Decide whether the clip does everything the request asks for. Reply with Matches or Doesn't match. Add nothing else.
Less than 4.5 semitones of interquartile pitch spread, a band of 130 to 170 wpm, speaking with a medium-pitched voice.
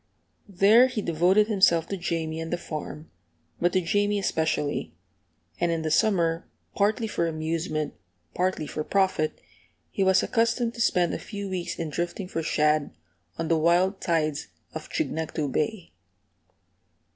Matches